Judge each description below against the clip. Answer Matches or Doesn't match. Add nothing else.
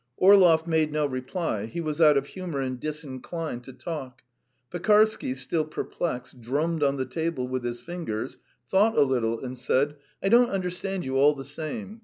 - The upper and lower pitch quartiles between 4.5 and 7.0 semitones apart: Matches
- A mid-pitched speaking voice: Matches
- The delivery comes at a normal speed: Matches